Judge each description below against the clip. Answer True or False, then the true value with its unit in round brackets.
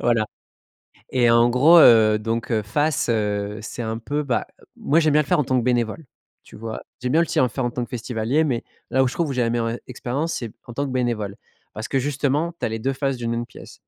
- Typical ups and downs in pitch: True (3.3 semitones)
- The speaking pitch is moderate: False (120 Hz)